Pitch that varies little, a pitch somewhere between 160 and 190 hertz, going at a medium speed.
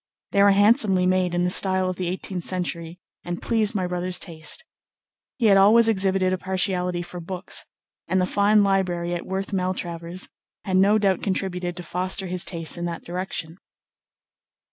Yes: narrow, 1.7 semitones; medium, 185 Hz; average, 170 wpm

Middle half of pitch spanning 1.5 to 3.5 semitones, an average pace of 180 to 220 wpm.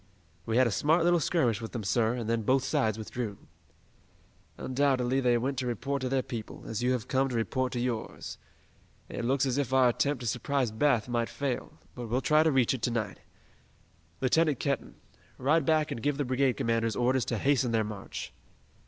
Yes: average, 2.9 semitones; average, 200 wpm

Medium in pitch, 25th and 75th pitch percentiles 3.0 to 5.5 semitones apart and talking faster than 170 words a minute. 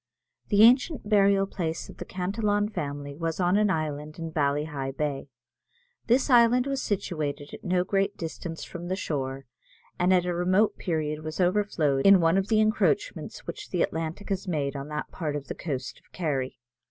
Yes: medium, 175 Hz; average, 4.9 semitones; average, 180 wpm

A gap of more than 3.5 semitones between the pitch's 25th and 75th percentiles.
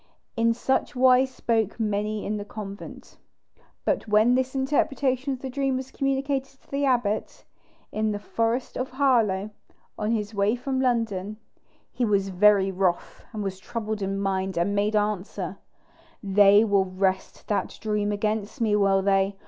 Yes: average, 4.0 semitones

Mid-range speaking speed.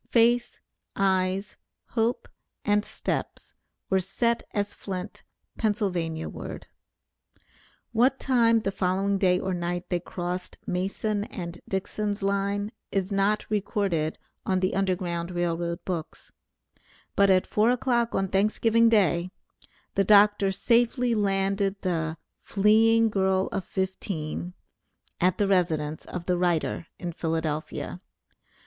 No: slow, 120 wpm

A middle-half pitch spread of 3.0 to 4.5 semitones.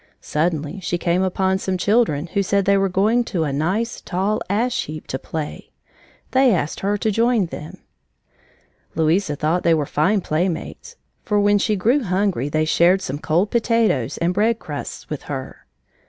No: average, 4.9 semitones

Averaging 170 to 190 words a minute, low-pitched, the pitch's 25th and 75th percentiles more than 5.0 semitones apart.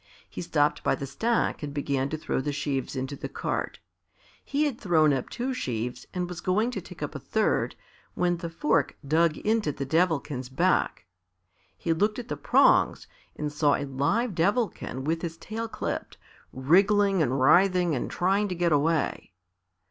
No: average, 175 wpm; medium, 165 Hz; wide, 5.5 semitones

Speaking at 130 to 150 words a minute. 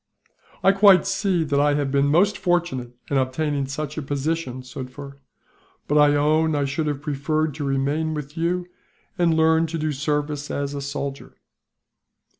No: average, 165 wpm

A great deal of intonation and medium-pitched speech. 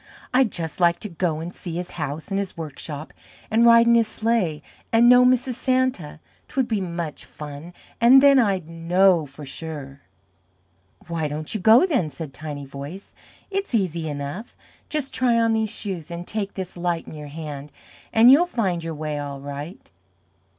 Yes: wide, 7.0 semitones; medium, 175 Hz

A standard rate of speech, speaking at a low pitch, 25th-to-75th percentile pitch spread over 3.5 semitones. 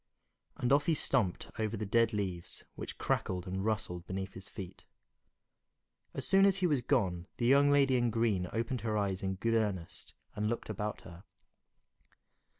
Yes: average, 170 wpm; low, 110 Hz; average, 4.2 semitones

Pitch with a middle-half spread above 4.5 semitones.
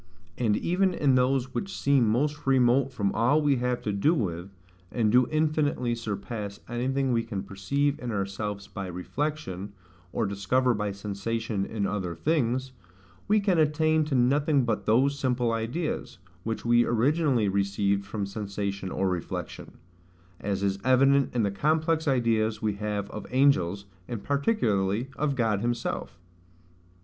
Yes: wide, 5.5 semitones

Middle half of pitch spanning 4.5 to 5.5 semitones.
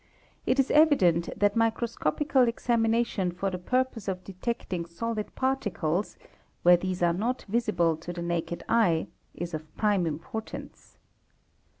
Yes: average, 5.2 semitones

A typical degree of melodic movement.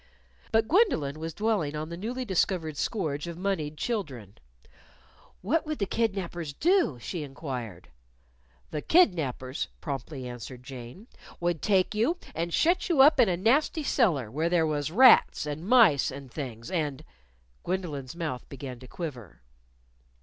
No: wide, 7.3 semitones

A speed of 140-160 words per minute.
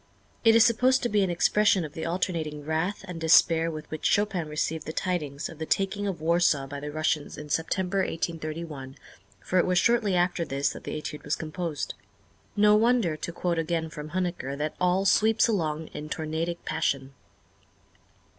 No: average, 180 wpm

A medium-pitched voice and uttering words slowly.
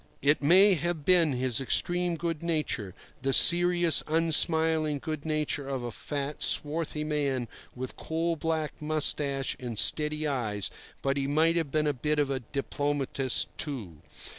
No: medium, 150 Hz; average, 150 wpm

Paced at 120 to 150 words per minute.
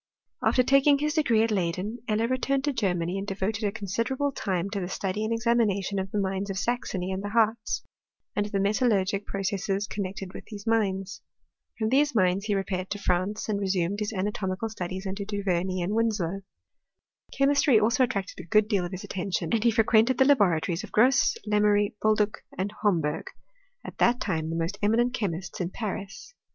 No: average, 195 wpm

